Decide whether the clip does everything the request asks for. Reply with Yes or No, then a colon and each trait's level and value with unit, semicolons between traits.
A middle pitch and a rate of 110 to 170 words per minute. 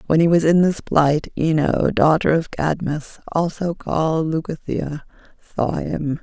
Yes: medium, 160 Hz; average, 145 wpm